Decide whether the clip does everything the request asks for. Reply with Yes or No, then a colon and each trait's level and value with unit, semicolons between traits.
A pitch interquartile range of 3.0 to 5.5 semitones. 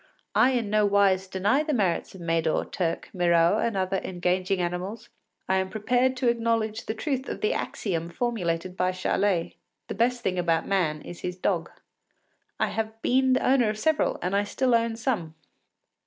Yes: average, 4.5 semitones